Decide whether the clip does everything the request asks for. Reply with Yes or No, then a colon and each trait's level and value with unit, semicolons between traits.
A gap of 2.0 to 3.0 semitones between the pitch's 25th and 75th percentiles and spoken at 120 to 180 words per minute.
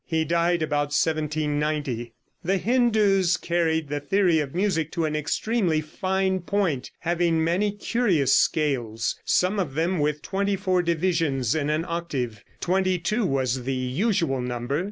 No: average, 4.3 semitones; average, 145 wpm